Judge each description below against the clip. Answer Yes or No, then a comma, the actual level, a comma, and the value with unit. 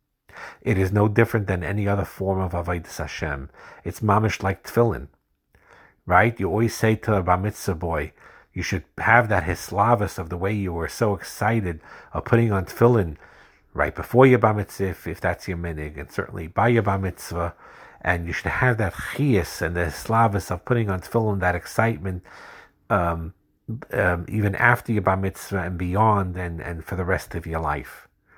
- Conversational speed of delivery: Yes, average, 185 wpm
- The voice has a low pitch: Yes, very low, 95 Hz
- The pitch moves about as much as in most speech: Yes, average, 3.8 semitones